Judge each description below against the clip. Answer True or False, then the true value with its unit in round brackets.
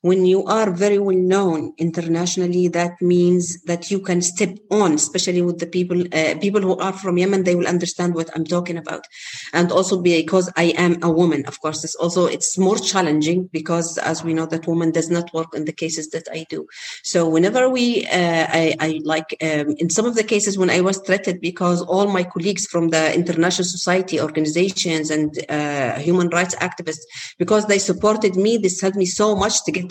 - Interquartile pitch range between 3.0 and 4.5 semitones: False (2.5 semitones)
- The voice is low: False (175 Hz)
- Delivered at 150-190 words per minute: False (205 wpm)